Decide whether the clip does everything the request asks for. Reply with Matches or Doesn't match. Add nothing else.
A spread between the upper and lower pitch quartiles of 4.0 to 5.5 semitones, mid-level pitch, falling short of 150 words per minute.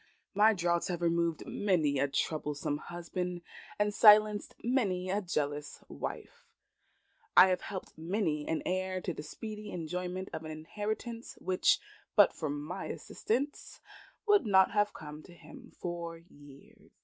Matches